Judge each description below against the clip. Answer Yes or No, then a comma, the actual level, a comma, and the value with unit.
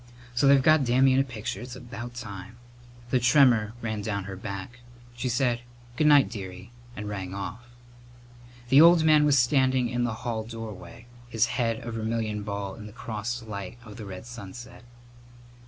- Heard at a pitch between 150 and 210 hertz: No, low, 115 Hz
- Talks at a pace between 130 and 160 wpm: No, average, 175 wpm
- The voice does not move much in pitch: No, average, 3.1 semitones